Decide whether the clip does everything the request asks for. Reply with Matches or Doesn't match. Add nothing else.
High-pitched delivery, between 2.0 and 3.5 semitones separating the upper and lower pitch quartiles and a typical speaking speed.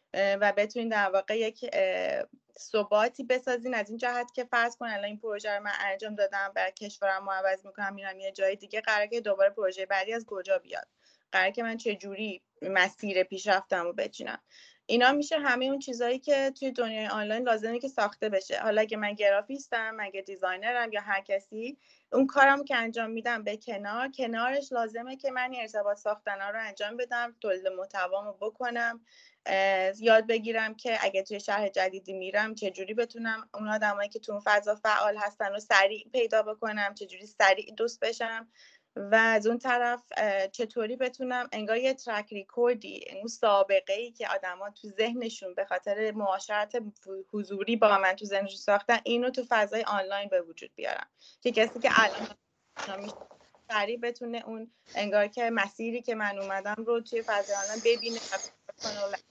Doesn't match